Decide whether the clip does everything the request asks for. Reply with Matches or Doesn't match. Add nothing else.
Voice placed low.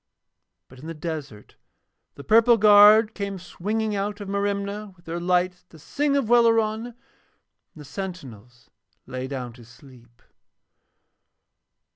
Doesn't match